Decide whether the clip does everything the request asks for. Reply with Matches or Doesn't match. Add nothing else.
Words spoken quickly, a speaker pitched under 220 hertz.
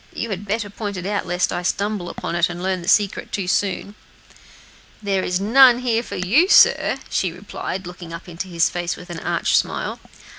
Matches